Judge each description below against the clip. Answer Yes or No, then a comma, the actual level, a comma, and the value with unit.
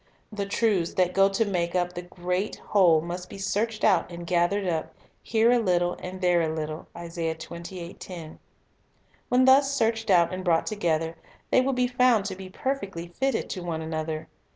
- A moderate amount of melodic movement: Yes, average, 3.7 semitones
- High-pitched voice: No, medium, 180 Hz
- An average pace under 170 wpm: No, average, 175 wpm